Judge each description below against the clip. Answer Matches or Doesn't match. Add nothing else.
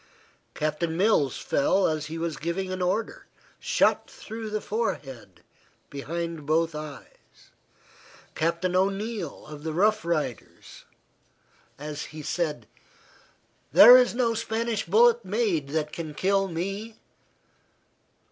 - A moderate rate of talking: Doesn't match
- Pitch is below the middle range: Doesn't match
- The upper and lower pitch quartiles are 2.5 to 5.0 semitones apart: Doesn't match